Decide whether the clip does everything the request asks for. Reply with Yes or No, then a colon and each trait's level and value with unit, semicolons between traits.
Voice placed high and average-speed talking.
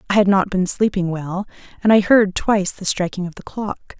No: high, 195 Hz; fast, 225 wpm